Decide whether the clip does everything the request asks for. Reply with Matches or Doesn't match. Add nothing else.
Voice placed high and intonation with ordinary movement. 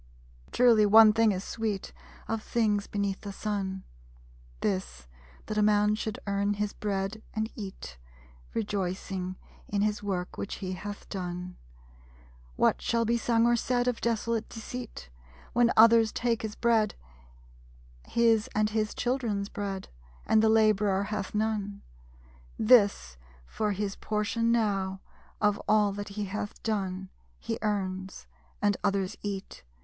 Doesn't match